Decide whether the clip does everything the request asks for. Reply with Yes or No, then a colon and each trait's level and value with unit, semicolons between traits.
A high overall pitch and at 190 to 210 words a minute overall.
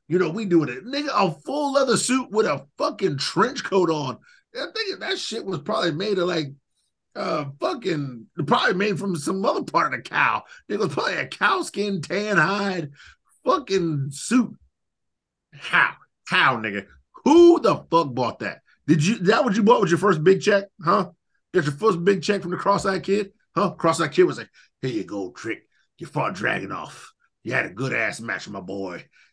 Yes: high, 195 Hz; average, 200 wpm